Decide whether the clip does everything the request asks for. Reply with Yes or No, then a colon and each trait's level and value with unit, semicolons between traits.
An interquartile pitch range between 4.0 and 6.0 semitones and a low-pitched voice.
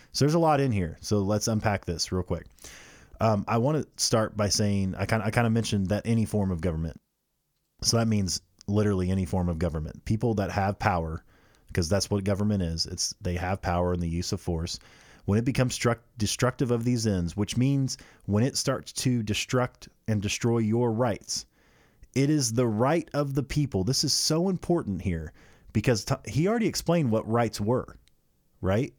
Yes: average, 4.8 semitones; low, 110 Hz